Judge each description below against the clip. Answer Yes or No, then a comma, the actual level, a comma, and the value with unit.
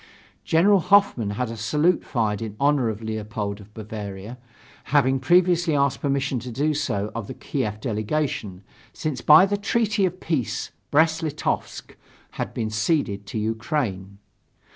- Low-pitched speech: Yes, low, 125 Hz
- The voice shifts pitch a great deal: Yes, wide, 6.4 semitones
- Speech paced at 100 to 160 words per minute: Yes, average, 145 wpm